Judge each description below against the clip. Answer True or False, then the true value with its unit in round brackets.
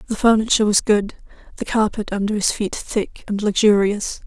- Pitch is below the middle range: False (210 Hz)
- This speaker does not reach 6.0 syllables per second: True (5.3 syllables/s)